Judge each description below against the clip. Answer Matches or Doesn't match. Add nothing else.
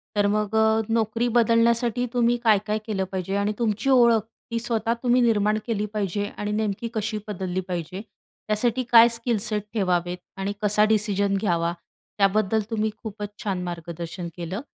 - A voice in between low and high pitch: Doesn't match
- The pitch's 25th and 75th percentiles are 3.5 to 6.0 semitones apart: Doesn't match